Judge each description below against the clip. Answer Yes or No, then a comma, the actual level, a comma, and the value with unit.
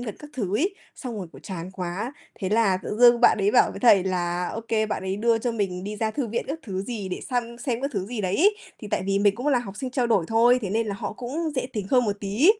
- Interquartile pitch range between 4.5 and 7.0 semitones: No, average, 3.9 semitones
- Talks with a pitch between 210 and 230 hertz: Yes, high, 220 Hz